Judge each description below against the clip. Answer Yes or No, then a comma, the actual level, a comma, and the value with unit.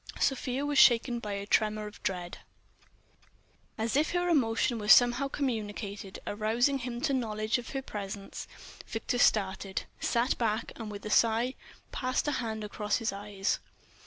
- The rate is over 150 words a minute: Yes, average, 160 wpm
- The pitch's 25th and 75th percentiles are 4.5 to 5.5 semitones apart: No, average, 3.2 semitones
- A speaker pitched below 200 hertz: No, high, 225 Hz